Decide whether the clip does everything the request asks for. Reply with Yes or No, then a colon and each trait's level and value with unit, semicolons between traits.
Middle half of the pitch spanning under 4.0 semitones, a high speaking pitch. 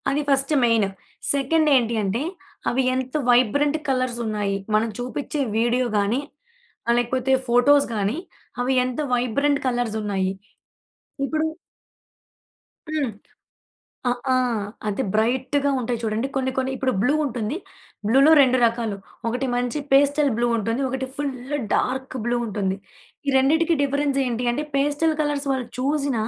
Yes: average, 3.1 semitones; very high, 255 Hz